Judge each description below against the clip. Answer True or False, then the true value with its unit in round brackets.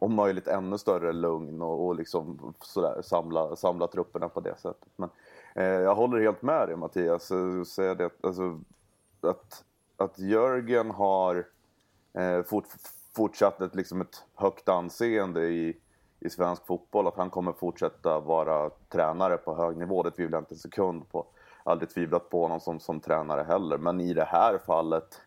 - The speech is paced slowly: False (170 wpm)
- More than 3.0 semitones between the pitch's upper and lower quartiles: False (2.5 semitones)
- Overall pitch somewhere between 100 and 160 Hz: False (90 Hz)